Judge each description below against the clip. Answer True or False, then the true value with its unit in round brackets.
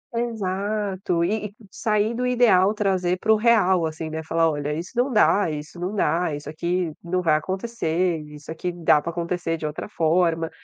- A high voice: False (180 Hz)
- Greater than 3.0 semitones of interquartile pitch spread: True (4.2 semitones)